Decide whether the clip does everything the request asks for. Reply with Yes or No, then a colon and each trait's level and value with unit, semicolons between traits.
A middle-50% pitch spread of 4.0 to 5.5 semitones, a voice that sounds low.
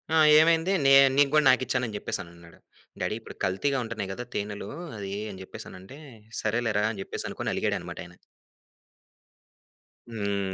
Yes: average, 4.9 semitones; low, 105 Hz